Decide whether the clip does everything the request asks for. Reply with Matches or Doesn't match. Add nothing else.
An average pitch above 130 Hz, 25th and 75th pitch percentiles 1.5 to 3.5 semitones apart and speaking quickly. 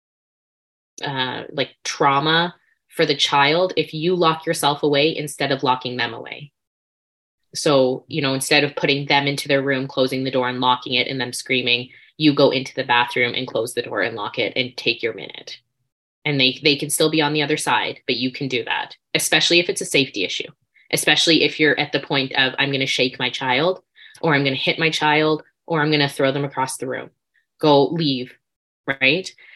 Matches